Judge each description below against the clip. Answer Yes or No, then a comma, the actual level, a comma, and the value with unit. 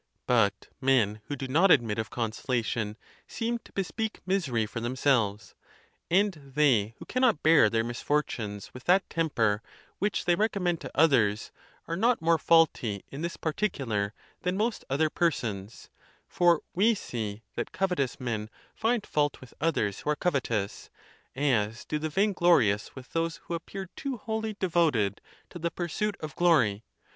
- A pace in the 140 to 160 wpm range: Yes, average, 155 wpm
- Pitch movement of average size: No, wide, 7.7 semitones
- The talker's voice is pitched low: No, medium, 150 Hz